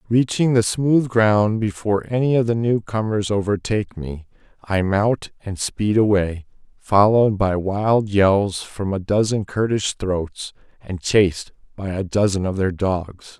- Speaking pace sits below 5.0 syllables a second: Yes, 4.1 syllables/s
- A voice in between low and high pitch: No, low, 105 Hz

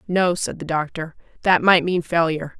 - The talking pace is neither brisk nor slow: Yes, average, 185 wpm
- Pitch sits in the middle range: Yes, medium, 170 Hz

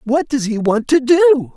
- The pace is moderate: No, fast, 230 wpm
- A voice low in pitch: No, very high, 265 Hz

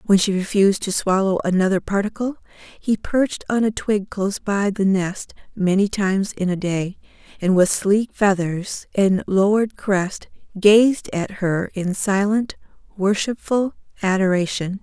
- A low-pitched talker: No, high, 200 Hz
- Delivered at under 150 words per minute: Yes, average, 140 wpm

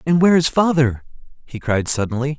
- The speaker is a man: Yes, male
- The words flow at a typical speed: Yes, average, 175 wpm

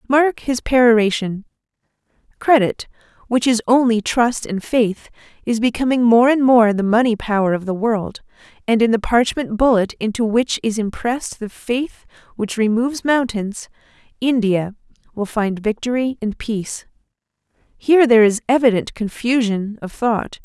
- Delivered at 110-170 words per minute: Yes, average, 140 wpm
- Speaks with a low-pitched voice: No, high, 230 Hz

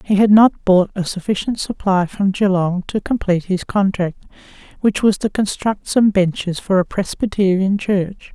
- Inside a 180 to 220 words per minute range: No, average, 165 wpm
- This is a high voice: Yes, high, 195 Hz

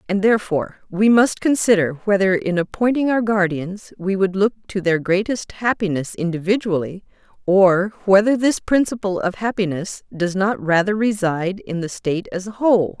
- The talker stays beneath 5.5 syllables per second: Yes, 5.0 syllables/s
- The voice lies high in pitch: Yes, high, 195 Hz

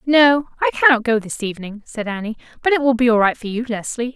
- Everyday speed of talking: No, fast, 245 wpm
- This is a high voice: Yes, high, 235 Hz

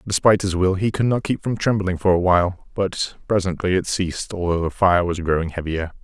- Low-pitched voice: Yes, very low, 95 Hz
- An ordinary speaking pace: No, fast, 220 wpm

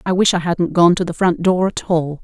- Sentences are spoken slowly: No, fast, 295 wpm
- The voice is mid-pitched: Yes, medium, 175 Hz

